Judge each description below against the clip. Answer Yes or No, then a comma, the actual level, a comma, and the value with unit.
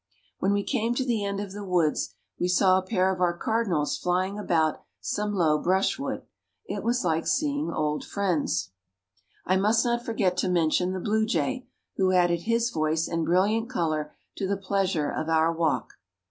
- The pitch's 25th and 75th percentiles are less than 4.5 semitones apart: Yes, average, 4.0 semitones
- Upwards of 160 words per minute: Yes, average, 180 wpm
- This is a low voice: No, medium, 185 Hz